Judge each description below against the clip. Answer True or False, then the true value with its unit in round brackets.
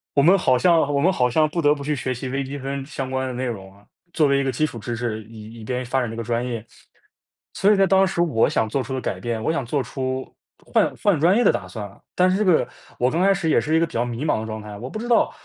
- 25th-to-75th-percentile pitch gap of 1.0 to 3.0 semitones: False (5.4 semitones)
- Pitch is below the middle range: True (130 Hz)